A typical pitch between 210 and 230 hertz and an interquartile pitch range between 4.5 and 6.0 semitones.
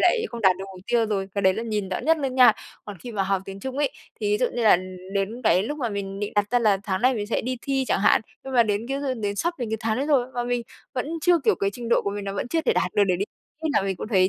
No: high, 220 Hz; average, 4.1 semitones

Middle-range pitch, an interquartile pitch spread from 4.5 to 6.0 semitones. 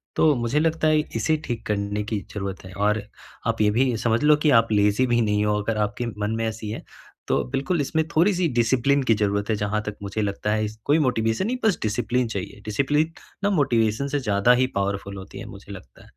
No: low, 110 Hz; average, 4.8 semitones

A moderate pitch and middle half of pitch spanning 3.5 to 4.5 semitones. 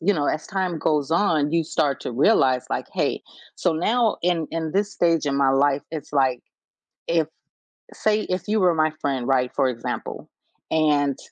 Yes: medium, 155 Hz; average, 4.1 semitones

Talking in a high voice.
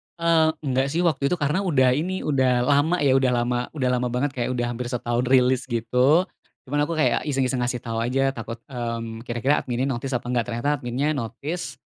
No: low, 130 Hz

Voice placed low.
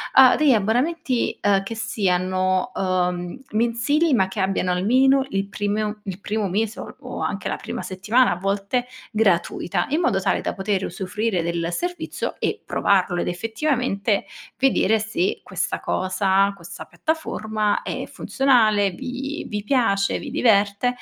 No: high, 210 Hz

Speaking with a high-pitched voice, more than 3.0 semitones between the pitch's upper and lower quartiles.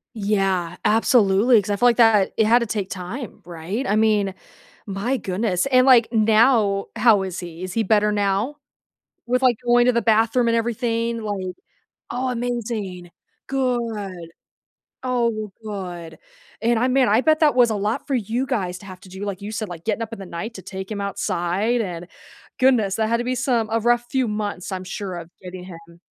Yes: high, 215 Hz; average, 3.8 semitones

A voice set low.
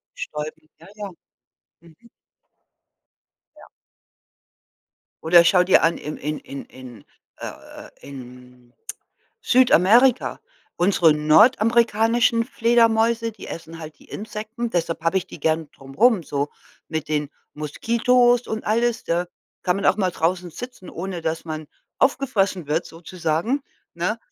No: medium, 180 Hz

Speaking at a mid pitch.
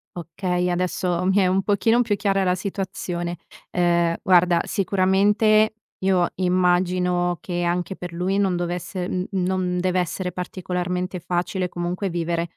Yes: medium, 180 Hz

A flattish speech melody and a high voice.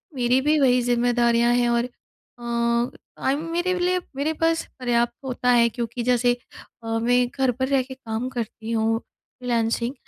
Yes: narrow, 1.8 semitones; high, 245 Hz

